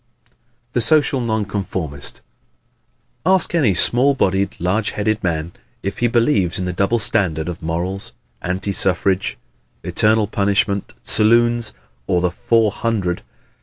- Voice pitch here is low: Yes, low, 100 Hz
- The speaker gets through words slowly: Yes, slow, 130 wpm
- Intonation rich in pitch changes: No, average, 4.1 semitones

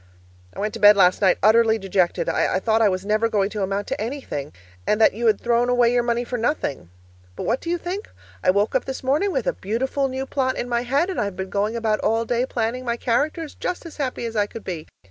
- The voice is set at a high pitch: Yes, high, 230 Hz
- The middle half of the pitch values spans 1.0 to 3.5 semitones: No, average, 4.0 semitones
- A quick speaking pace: Yes, fast, 250 wpm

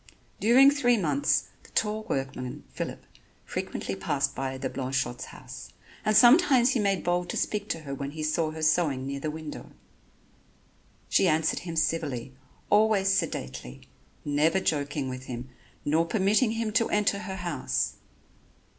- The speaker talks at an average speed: Yes, average, 150 wpm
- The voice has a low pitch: No, medium, 160 Hz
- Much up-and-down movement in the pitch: Yes, wide, 7.1 semitones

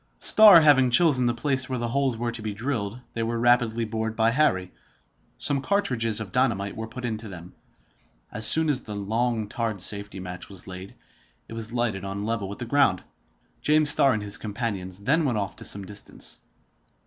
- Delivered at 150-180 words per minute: No, average, 195 wpm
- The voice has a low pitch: Yes, low, 115 Hz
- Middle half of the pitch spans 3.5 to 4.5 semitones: Yes, average, 3.9 semitones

